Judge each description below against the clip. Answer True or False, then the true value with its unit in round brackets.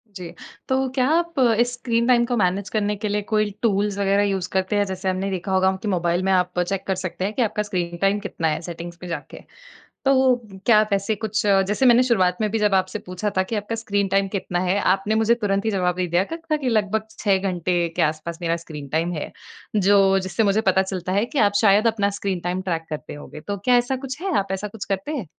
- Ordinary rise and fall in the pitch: True (3.0 semitones)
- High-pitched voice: True (195 Hz)